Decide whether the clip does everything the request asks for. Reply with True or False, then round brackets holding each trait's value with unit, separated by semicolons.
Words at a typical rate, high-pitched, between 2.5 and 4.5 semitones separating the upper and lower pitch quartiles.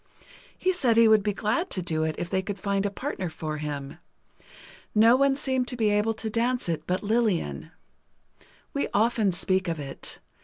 False (190 wpm; 205 Hz; 5.2 semitones)